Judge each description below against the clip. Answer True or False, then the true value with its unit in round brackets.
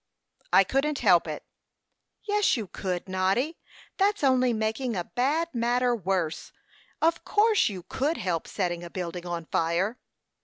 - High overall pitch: True (220 Hz)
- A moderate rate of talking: True (145 wpm)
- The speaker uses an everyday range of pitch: False (7.3 semitones)